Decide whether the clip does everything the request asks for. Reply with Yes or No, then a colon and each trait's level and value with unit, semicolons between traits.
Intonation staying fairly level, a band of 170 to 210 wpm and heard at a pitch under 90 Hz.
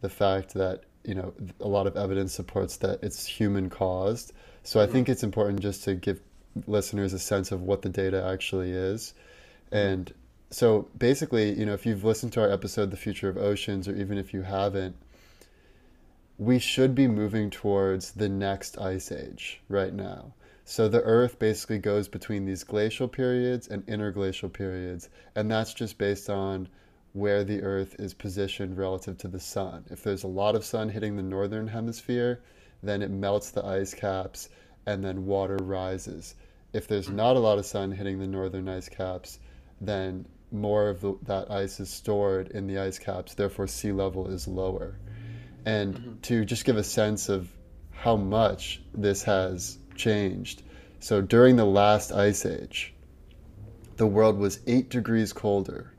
No: narrow, 2.0 semitones; average, 175 wpm; low, 100 Hz